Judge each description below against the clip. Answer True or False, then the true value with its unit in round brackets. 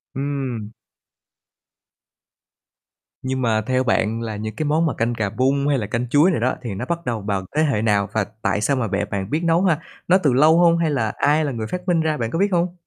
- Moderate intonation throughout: False (6.3 semitones)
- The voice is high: False (130 Hz)